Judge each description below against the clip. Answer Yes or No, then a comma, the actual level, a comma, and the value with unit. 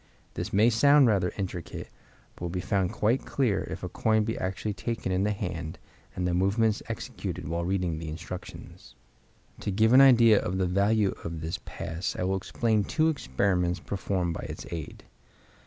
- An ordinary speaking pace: Yes, average, 180 wpm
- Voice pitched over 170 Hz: No, very low, 95 Hz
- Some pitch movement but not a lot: Yes, average, 3.7 semitones